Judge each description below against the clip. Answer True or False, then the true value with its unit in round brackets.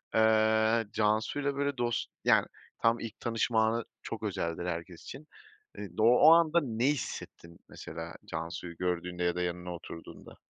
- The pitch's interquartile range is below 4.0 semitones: False (5.2 semitones)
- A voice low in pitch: True (110 Hz)